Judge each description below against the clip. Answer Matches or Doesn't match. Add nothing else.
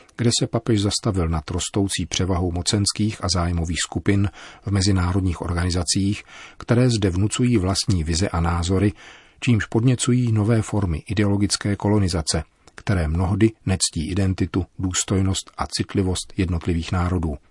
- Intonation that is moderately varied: Matches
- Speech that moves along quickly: Doesn't match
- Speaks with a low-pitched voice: Matches